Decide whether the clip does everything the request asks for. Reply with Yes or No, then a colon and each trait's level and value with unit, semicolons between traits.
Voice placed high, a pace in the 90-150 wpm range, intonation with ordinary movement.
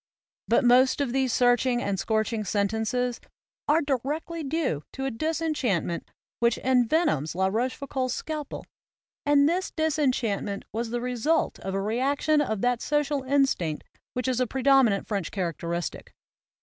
Yes: very high, 250 Hz; average, 145 wpm; average, 4.6 semitones